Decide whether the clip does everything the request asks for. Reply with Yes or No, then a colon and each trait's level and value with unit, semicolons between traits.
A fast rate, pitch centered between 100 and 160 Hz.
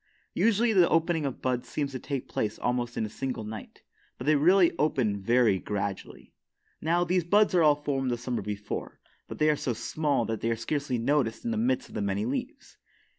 Yes: fast, 210 wpm; low, 135 Hz